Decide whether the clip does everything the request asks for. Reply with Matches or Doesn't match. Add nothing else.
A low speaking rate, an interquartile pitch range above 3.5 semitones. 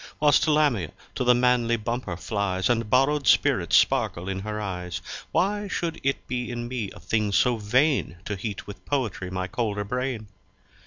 Doesn't match